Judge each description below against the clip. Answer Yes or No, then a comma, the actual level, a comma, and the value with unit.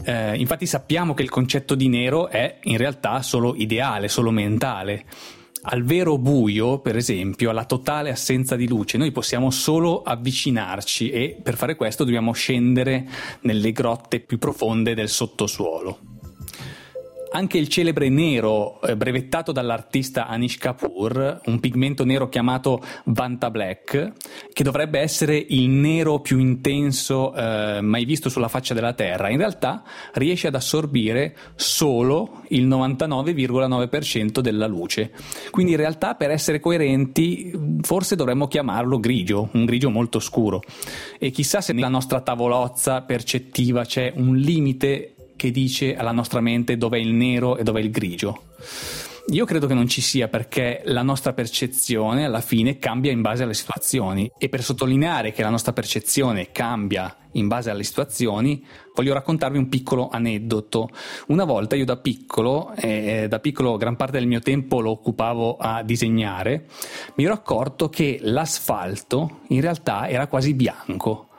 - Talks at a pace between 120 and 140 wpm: No, average, 150 wpm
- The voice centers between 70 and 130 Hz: Yes, low, 125 Hz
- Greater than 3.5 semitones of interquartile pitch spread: No, average, 3.1 semitones